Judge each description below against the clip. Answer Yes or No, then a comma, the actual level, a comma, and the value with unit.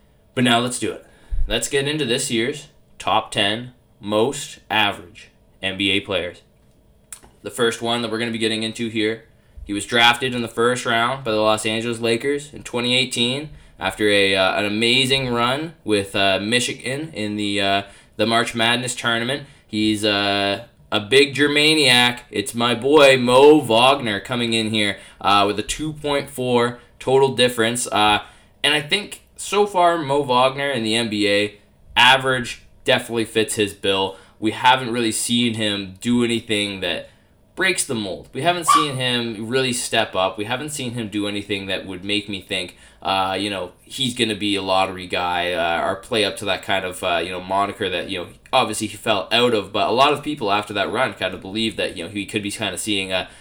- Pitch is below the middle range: Yes, low, 110 Hz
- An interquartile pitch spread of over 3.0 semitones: Yes, average, 3.5 semitones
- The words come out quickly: No, average, 195 wpm